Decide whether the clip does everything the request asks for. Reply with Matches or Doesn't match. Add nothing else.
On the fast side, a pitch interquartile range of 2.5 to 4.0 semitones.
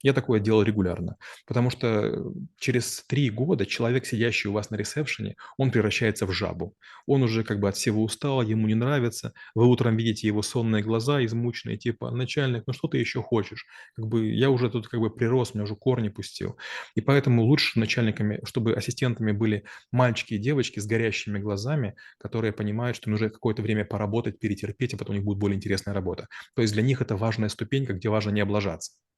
Matches